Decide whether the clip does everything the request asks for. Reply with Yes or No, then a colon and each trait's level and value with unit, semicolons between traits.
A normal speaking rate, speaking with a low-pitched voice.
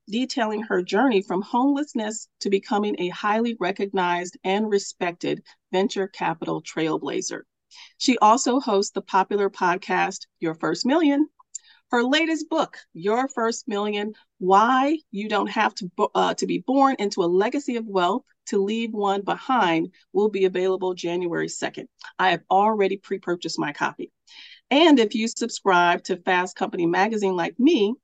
No: average, 150 wpm; high, 205 Hz